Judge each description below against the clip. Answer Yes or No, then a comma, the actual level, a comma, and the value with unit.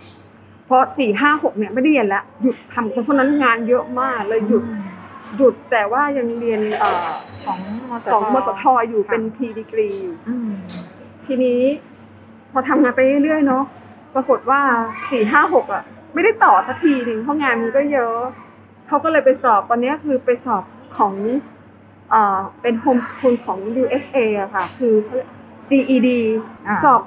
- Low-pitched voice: No, very high, 250 Hz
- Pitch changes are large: No, average, 3.4 semitones